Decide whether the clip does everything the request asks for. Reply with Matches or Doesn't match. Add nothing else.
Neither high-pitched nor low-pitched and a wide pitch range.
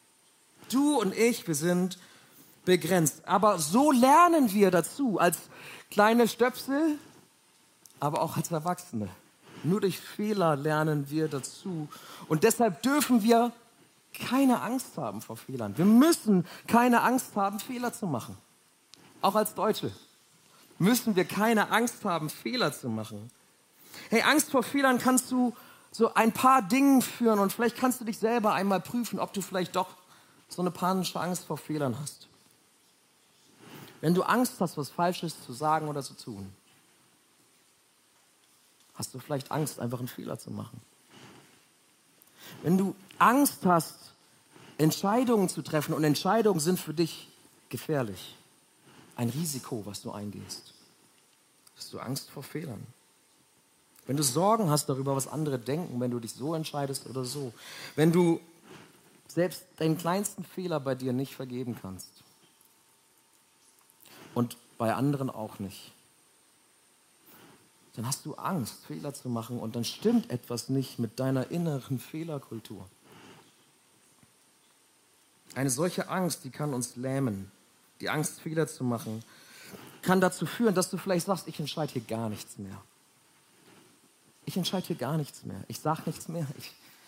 Matches